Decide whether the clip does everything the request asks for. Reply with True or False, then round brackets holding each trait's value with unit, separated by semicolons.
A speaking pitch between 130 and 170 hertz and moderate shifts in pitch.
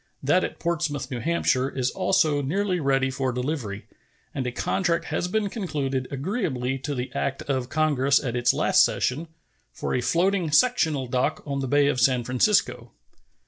True (140 Hz; 4.6 semitones)